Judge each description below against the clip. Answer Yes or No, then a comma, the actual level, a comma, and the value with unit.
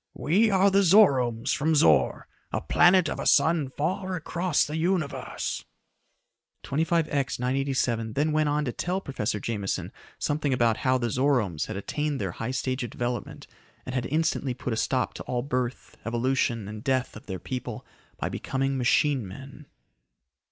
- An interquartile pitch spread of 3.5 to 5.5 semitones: Yes, average, 4.3 semitones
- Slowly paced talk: No, average, 160 wpm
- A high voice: No, low, 135 Hz